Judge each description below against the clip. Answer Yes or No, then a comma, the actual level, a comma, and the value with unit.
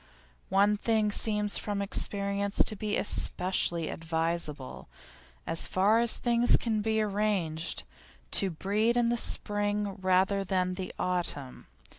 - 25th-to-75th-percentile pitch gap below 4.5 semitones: Yes, narrow, 2.5 semitones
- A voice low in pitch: No, high, 200 Hz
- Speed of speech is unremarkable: No, slow, 115 wpm